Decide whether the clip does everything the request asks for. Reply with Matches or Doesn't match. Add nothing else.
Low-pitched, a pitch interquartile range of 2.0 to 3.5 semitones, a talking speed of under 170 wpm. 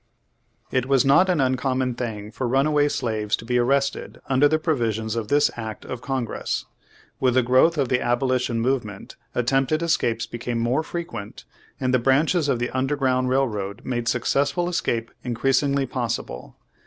Matches